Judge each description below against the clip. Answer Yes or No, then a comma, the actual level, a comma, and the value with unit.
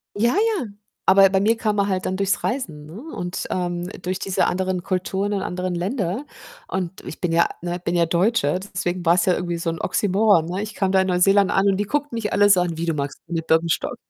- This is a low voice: No, medium, 185 Hz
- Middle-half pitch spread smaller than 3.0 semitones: Yes, narrow, 2.6 semitones